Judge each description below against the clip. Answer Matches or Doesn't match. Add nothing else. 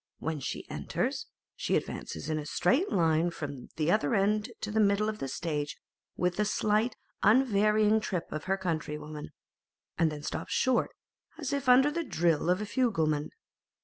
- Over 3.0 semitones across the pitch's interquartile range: Matches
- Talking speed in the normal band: Matches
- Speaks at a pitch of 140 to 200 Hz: Matches